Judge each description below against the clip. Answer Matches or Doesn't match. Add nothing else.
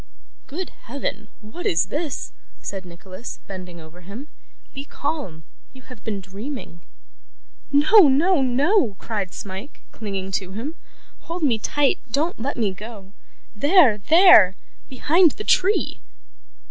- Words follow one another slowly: Matches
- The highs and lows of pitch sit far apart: Matches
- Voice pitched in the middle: Doesn't match